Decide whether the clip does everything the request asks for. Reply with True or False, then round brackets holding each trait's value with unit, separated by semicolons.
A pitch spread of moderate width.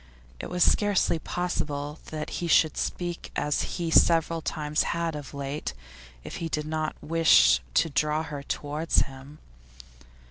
False (2.1 semitones)